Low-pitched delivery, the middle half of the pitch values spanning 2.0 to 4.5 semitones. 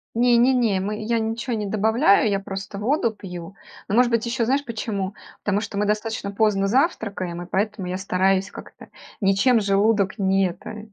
No: high, 210 Hz; narrow, 2.6 semitones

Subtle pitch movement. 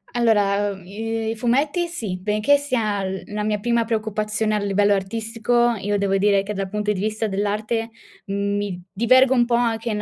Yes: narrow, 2.3 semitones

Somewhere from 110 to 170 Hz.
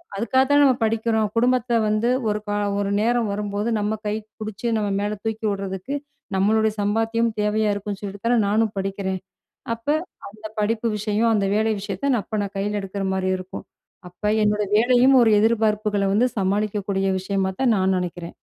No: high, 210 Hz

